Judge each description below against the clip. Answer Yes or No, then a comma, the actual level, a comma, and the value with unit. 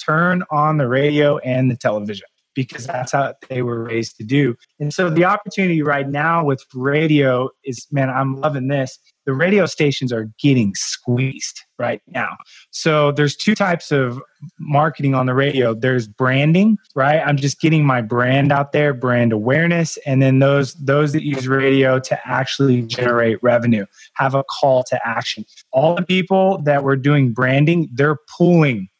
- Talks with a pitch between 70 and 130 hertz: No, medium, 140 Hz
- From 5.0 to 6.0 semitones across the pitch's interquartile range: No, average, 3.0 semitones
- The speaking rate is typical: Yes, average, 170 wpm